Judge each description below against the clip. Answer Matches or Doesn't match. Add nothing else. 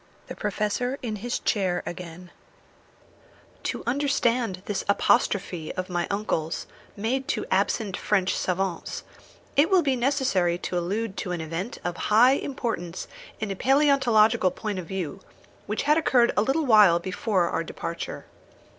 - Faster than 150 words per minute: Doesn't match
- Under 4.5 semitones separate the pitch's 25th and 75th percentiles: Doesn't match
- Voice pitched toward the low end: Doesn't match